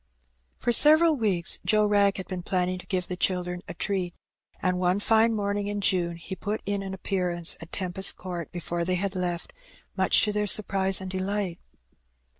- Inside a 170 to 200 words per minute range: Yes, average, 185 wpm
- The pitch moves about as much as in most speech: No, narrow, 2.3 semitones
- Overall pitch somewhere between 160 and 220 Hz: Yes, high, 190 Hz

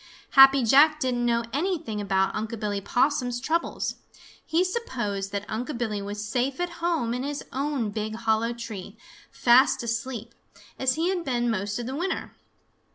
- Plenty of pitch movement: No, average, 4.4 semitones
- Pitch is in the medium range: No, high, 240 Hz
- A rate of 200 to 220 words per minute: No, average, 160 wpm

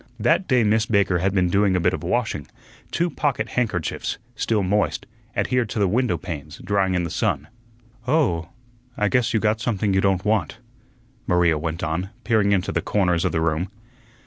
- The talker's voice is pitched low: Yes, low, 100 Hz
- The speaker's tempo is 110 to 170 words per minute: No, average, 185 wpm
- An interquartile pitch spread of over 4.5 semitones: No, average, 4.0 semitones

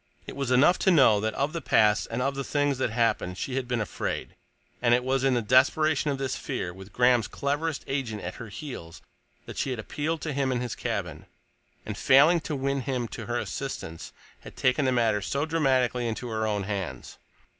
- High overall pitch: No, low, 130 Hz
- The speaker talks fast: Yes, fast, 210 wpm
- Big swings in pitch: No, average, 3.8 semitones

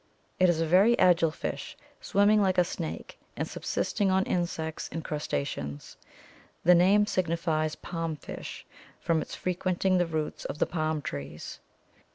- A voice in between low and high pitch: Yes, medium, 170 Hz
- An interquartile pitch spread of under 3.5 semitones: Yes, average, 2.8 semitones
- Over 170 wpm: No, average, 150 wpm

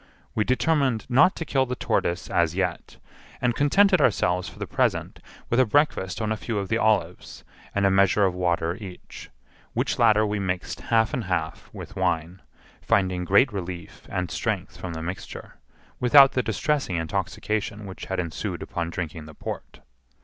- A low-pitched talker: Yes, low, 100 Hz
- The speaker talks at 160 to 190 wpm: Yes, average, 170 wpm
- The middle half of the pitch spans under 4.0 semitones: No, average, 4.9 semitones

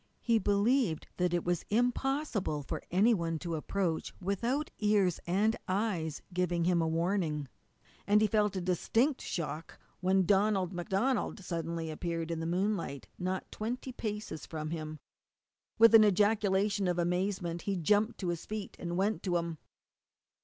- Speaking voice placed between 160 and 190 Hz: Yes, medium, 185 Hz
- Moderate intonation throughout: Yes, average, 3.8 semitones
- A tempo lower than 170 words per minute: Yes, average, 150 wpm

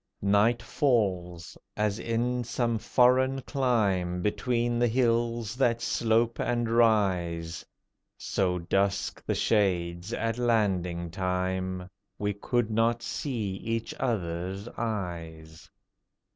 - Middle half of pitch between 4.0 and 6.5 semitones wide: Yes, average, 4.4 semitones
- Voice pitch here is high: No, low, 110 Hz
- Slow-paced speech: Yes, slow, 105 wpm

